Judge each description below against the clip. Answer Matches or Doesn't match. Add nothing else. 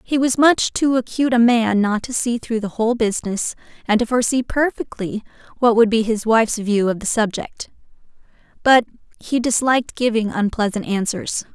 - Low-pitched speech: Doesn't match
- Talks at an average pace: Matches